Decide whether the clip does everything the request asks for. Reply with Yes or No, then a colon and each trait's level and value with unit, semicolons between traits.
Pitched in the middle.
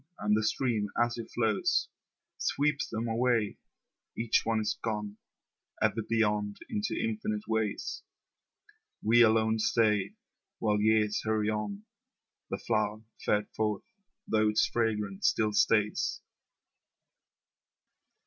No: low, 110 Hz